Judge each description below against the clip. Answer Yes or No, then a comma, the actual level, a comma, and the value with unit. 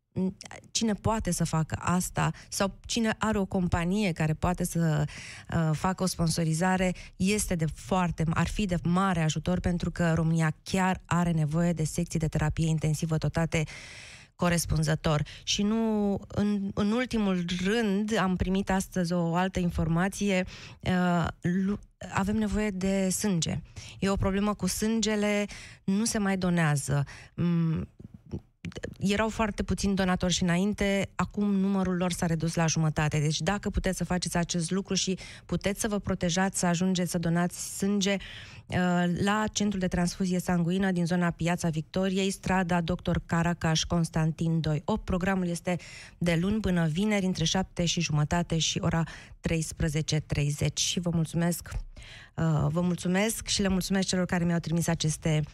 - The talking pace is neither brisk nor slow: Yes, average, 150 wpm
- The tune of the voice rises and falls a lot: No, average, 2.9 semitones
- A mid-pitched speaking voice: Yes, medium, 175 Hz